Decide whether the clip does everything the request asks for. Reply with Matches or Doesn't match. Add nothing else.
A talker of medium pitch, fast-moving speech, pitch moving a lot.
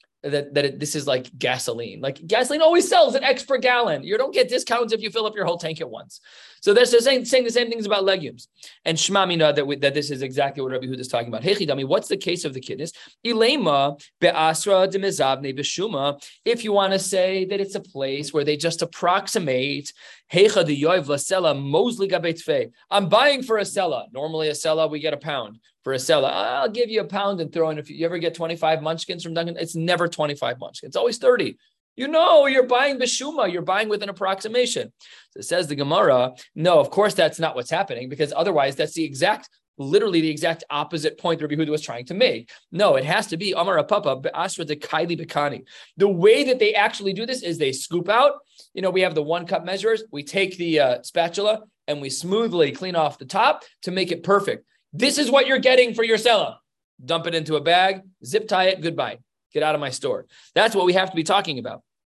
Matches